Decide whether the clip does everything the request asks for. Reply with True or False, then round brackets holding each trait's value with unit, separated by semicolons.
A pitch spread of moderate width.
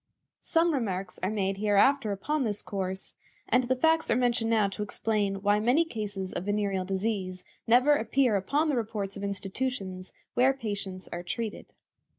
True (4.3 semitones)